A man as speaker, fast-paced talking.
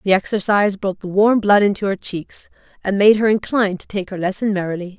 No: female; fast, 215 wpm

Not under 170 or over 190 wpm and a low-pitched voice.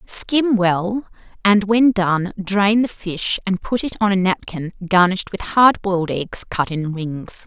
No: average, 175 wpm; high, 195 Hz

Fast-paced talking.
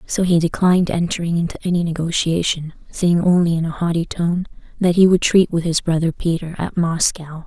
No: average, 185 wpm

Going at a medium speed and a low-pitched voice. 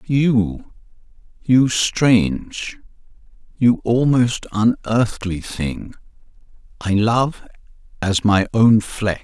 No: slow, 70 wpm; low, 110 Hz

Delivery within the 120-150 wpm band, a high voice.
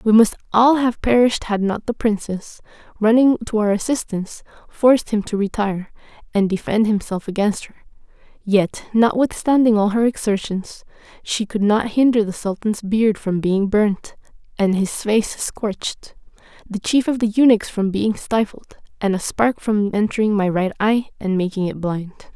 No: average, 165 wpm; high, 210 Hz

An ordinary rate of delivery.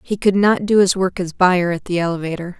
No: fast, 255 wpm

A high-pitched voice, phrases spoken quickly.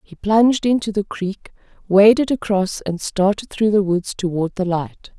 No: high, 200 Hz; average, 175 wpm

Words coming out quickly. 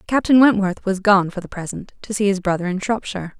Yes: fast, 230 wpm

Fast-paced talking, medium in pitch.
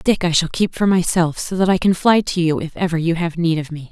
Yes: fast, 320 wpm; medium, 170 Hz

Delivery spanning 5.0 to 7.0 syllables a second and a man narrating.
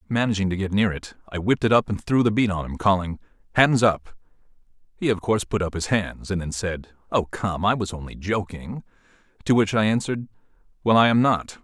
Yes: 5.8 syllables/s; male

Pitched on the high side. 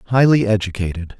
No: low, 105 Hz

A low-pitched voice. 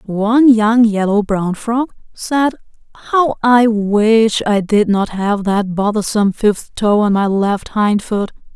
No: high, 215 Hz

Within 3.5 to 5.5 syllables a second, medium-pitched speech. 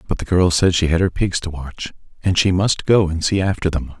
No: 5.4 syllables/s; very low, 90 Hz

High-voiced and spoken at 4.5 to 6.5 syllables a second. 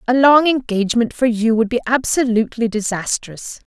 Yes: high, 235 Hz; 5.3 syllables/s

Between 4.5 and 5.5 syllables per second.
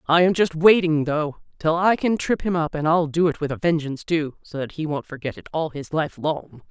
Yes: 5.3 syllables/s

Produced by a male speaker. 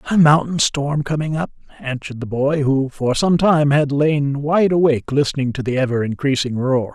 Yes: male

